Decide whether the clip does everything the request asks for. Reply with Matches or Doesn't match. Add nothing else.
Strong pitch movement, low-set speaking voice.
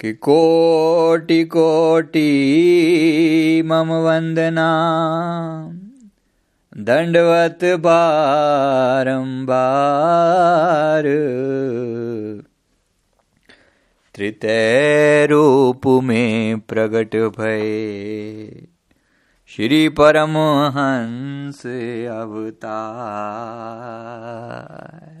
Doesn't match